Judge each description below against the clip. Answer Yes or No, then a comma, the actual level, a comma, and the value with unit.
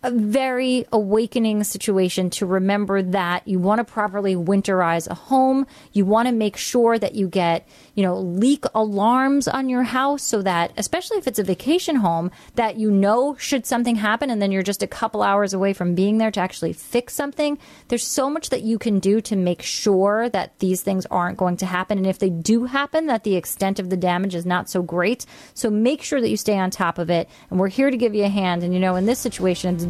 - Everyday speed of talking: No, fast, 230 wpm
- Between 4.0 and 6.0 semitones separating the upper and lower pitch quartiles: Yes, average, 4.5 semitones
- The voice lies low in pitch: No, high, 210 Hz